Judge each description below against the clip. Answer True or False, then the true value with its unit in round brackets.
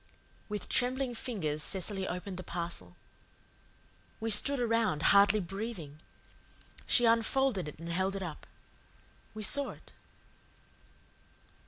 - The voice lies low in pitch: False (200 Hz)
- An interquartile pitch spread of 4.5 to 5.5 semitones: True (4.9 semitones)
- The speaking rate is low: True (115 wpm)